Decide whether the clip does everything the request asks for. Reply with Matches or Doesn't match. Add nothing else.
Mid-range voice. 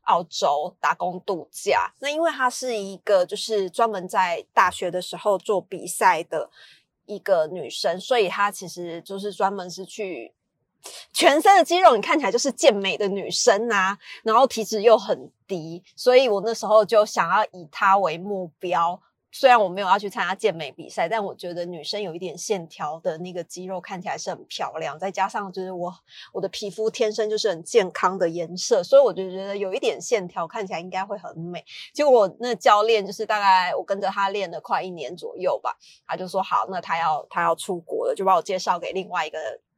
Doesn't match